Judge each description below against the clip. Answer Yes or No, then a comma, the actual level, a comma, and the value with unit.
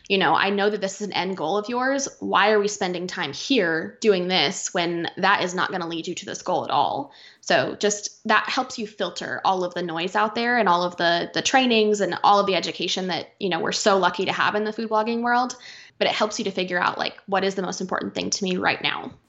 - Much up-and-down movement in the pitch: No, average, 3.1 semitones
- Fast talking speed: Yes, fast, 270 wpm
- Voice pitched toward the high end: Yes, high, 200 Hz